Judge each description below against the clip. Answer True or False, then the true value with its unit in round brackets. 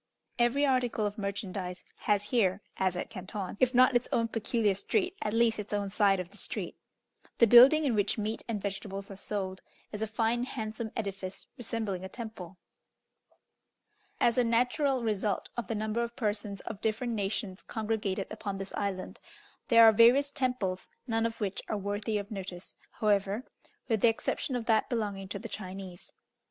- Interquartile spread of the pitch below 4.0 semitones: True (2.9 semitones)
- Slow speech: False (175 wpm)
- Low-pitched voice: False (215 Hz)